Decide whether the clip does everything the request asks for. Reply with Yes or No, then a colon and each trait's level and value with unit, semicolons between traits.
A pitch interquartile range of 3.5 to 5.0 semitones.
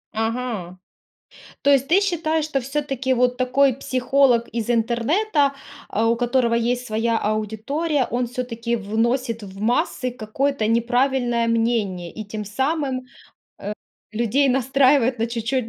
No: average, 3.1 semitones